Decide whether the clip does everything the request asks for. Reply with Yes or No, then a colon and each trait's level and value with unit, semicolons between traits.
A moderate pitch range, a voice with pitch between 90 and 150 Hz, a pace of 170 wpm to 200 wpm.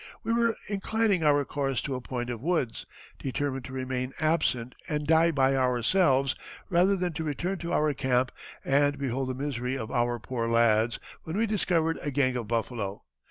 Yes: average, 4.6 semitones; low, 135 Hz; average, 180 wpm